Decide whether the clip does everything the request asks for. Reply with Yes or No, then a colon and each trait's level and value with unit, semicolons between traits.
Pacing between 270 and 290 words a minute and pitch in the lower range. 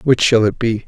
Yes: fast, 275 wpm; low, 115 Hz